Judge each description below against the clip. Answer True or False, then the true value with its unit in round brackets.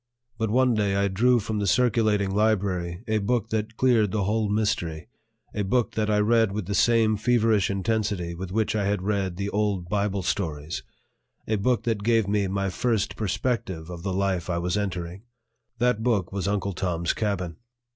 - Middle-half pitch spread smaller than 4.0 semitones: True (2.7 semitones)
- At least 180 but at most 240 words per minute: True (185 wpm)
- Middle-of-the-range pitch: False (100 Hz)